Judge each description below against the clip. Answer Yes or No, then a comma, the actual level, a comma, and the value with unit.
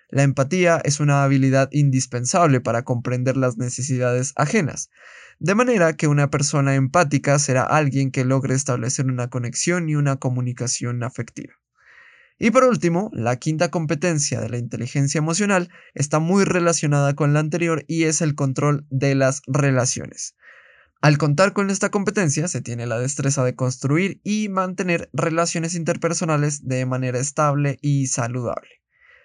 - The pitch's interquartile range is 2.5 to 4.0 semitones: No, average, 4.4 semitones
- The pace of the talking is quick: No, average, 145 wpm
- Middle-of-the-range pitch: Yes, medium, 145 Hz